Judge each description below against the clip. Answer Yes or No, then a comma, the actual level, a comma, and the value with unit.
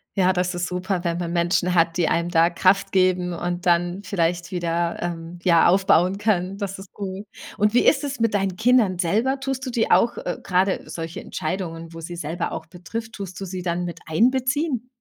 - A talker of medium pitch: Yes, medium, 180 Hz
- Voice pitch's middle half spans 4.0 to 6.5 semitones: No, average, 2.7 semitones